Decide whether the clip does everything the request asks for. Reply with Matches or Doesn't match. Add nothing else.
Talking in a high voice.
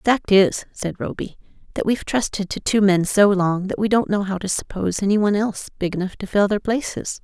Matches